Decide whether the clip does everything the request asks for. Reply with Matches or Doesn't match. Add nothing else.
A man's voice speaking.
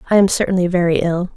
Doesn't match